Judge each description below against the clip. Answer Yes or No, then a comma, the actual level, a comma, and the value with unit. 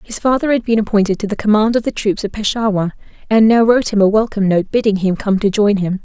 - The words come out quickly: Yes, fast, 260 wpm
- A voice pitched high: Yes, high, 210 Hz